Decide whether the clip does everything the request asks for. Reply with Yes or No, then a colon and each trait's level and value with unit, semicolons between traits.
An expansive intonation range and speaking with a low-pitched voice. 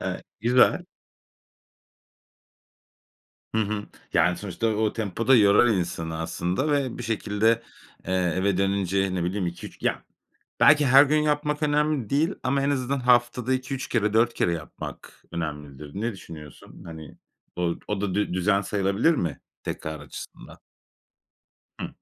Yes: wide, 6.2 semitones; low, 105 Hz